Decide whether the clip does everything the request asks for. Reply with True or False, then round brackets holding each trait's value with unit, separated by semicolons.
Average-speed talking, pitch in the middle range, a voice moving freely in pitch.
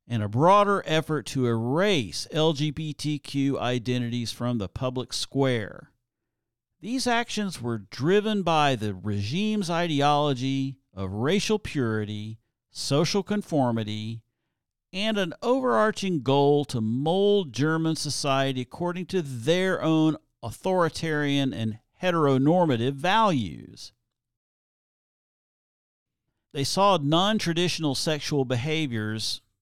False (95 wpm; 145 Hz; 6.1 semitones)